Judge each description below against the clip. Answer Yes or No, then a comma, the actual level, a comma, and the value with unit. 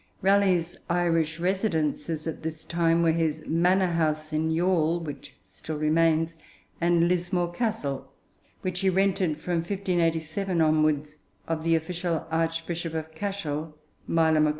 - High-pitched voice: No, medium, 165 Hz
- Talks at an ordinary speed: No, slow, 130 wpm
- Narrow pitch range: Yes, narrow, 2.0 semitones